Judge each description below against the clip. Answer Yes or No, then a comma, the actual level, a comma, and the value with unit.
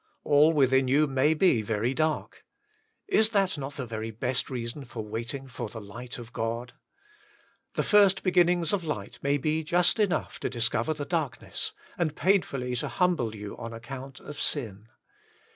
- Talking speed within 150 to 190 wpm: Yes, average, 165 wpm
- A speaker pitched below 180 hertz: Yes, low, 135 Hz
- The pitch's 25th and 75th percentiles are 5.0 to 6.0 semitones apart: Yes, wide, 5.4 semitones